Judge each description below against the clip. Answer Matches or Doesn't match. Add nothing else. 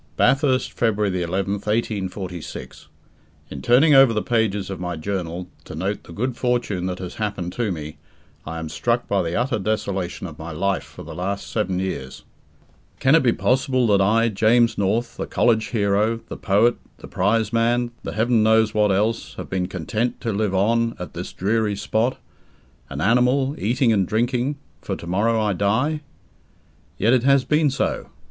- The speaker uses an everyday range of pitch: Matches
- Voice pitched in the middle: Doesn't match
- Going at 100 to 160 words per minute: Doesn't match